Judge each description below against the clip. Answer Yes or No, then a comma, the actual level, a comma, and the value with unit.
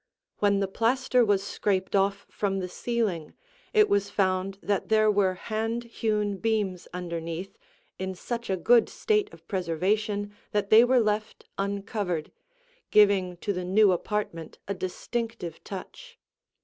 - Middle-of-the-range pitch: No, high, 200 Hz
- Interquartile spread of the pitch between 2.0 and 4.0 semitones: Yes, average, 2.8 semitones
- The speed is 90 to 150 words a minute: Yes, average, 140 wpm